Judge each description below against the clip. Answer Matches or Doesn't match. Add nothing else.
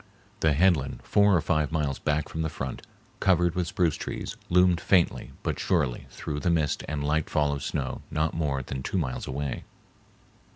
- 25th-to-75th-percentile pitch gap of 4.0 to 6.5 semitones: Doesn't match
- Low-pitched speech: Matches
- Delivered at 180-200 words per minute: Matches